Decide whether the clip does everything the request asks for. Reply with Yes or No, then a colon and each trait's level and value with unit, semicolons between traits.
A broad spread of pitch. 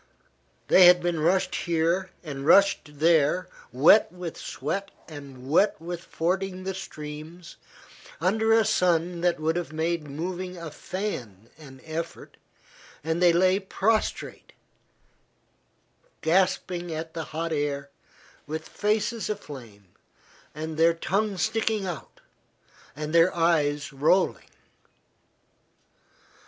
No: average, 3.3 semitones